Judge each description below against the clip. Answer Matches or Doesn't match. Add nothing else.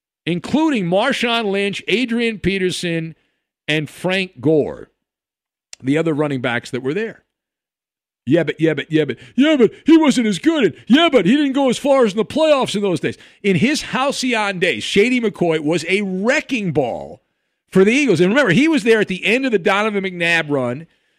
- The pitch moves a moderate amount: Doesn't match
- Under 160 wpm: Doesn't match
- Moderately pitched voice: Doesn't match